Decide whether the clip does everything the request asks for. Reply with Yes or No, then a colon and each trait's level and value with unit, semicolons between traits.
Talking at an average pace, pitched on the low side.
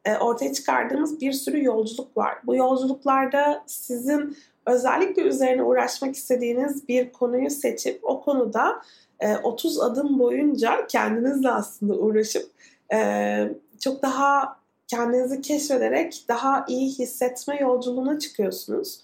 No: average, 105 wpm; very high, 265 Hz